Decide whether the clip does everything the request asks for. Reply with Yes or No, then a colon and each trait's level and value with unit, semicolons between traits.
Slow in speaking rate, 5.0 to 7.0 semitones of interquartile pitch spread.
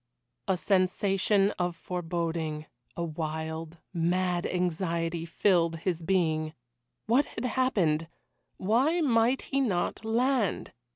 No: slow, 105 wpm; average, 4.3 semitones